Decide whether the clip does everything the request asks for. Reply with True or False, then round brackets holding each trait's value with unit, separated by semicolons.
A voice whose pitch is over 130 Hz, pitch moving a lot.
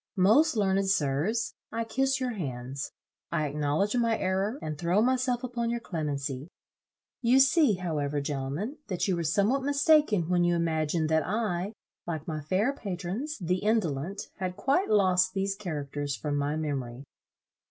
True (185 Hz; 7.1 semitones)